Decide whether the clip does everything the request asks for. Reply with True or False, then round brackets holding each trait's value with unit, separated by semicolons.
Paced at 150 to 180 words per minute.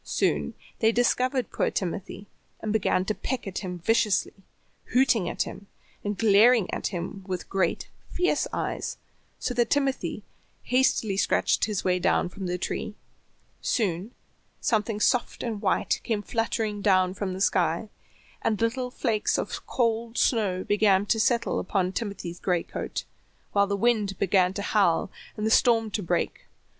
True (155 wpm)